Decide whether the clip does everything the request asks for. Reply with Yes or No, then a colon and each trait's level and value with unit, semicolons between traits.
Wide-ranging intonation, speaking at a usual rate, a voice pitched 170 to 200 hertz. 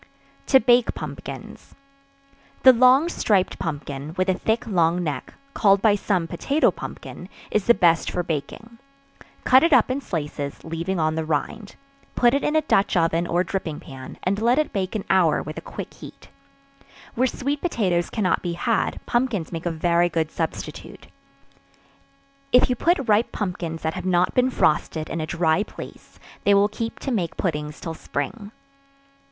Yes: wide, 6.2 semitones; average, 170 wpm; medium, 185 Hz